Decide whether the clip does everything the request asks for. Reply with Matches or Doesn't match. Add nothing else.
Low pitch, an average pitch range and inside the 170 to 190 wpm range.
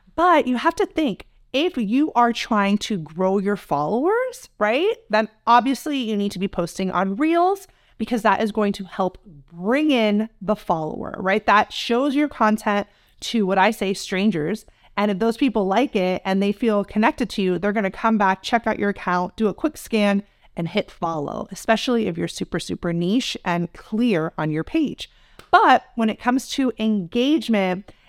Doesn't match